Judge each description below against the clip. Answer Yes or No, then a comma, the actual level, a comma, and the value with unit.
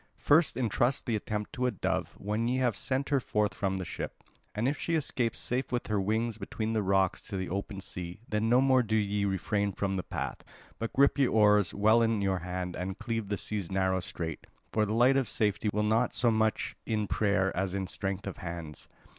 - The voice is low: Yes, low, 105 Hz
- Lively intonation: No, average, 3.3 semitones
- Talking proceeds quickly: Yes, fast, 220 wpm